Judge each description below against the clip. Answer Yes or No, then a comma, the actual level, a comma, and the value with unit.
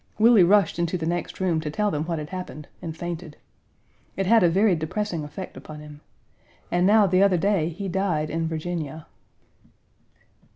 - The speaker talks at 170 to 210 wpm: Yes, average, 175 wpm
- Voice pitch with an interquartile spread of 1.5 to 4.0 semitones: Yes, average, 3.4 semitones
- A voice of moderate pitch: Yes, medium, 175 Hz